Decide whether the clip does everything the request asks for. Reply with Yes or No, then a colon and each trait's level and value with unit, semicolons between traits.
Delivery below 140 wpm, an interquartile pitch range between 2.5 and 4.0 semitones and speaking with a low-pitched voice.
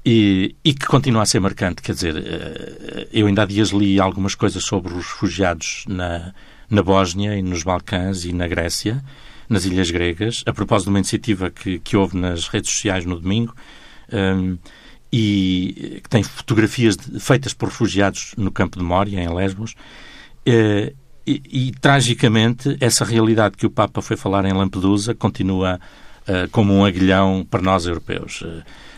No: average, 160 wpm; average, 3.1 semitones; low, 100 Hz